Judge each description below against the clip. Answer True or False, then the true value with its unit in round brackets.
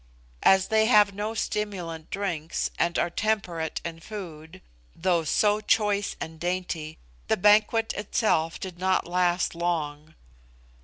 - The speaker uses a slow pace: True (125 wpm)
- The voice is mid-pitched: True (180 Hz)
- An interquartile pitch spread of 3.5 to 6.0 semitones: True (4.0 semitones)